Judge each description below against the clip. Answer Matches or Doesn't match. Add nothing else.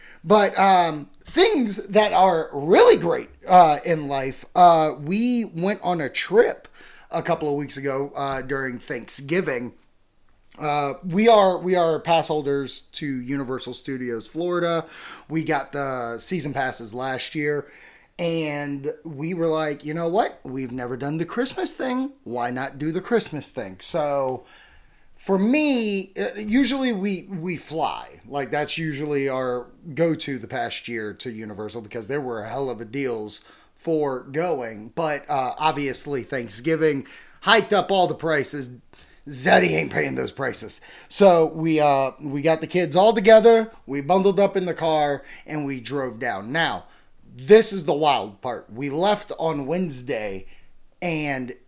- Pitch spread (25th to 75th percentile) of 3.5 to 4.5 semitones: Doesn't match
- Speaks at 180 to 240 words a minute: Doesn't match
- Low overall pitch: Doesn't match